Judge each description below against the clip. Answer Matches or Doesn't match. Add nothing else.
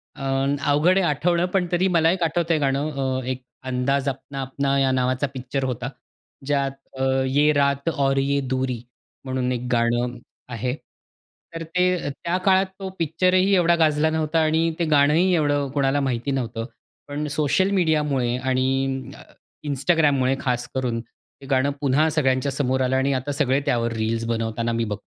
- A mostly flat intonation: Doesn't match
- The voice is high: Doesn't match